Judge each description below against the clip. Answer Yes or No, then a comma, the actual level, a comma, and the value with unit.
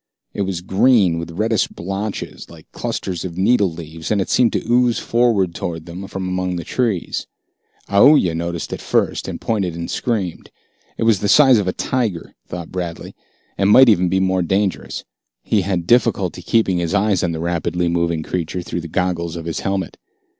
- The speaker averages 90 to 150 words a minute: No, average, 185 wpm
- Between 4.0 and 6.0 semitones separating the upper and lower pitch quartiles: No, average, 3.5 semitones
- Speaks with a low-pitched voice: Yes, very low, 95 Hz